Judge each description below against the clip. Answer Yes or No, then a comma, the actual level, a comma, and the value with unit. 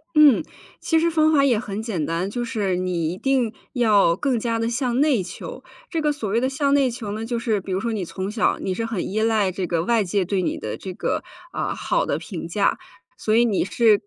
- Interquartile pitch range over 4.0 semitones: Yes, average, 4.6 semitones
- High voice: Yes, high, 220 Hz